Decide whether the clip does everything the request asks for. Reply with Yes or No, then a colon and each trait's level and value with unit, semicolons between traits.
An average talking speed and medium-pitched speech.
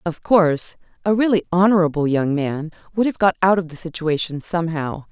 Yes: average, 175 wpm; medium, 170 Hz